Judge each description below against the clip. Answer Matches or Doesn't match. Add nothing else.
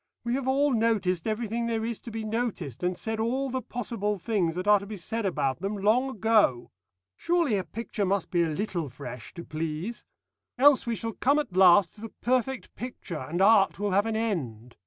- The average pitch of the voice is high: Matches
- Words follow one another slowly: Doesn't match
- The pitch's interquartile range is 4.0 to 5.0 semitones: Matches